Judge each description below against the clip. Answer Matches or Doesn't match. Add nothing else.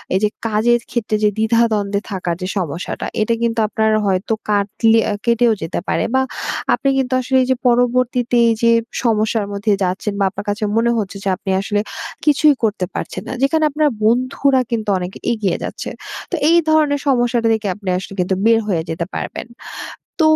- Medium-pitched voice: Doesn't match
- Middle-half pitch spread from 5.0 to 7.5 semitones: Doesn't match